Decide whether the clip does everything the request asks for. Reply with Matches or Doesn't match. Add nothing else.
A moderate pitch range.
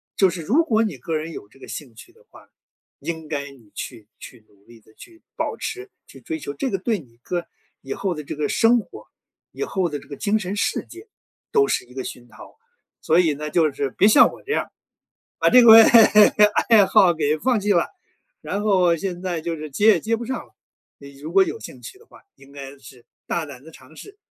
Doesn't match